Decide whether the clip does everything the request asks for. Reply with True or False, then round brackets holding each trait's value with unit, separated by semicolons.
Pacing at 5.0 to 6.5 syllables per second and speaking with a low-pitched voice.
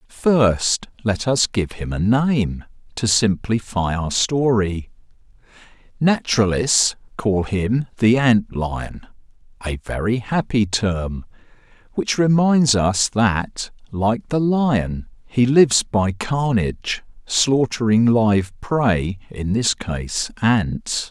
False (3.2 syllables/s; 110 Hz)